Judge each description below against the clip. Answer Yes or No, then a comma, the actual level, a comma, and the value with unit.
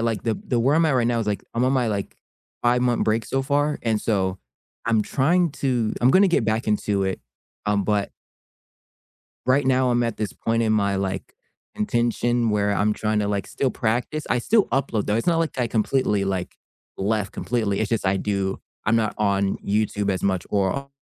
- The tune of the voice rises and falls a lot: No, average, 3.5 semitones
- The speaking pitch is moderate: No, low, 110 Hz